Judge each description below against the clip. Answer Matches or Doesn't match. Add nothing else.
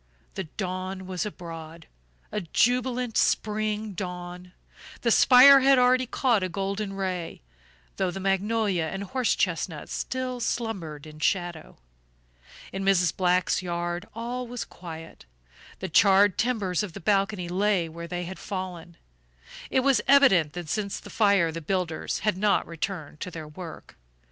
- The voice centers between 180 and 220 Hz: Matches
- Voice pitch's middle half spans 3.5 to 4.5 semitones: Matches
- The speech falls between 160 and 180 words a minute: Doesn't match